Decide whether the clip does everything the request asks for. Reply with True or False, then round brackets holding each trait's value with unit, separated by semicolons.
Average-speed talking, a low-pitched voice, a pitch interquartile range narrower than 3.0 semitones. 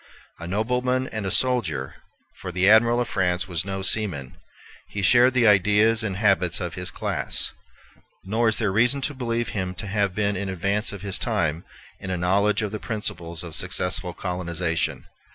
False (180 wpm; 100 Hz; 3.6 semitones)